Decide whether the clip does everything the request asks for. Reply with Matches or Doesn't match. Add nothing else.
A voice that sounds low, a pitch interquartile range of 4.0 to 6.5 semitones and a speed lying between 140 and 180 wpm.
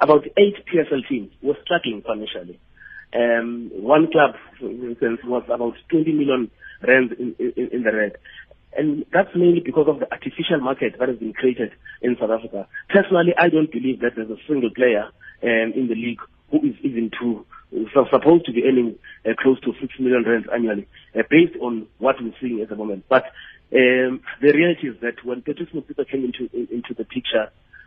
Doesn't match